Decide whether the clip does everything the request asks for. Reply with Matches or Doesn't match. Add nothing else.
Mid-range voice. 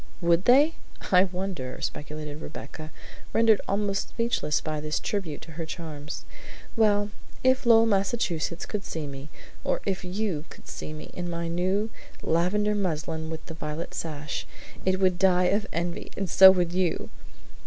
Matches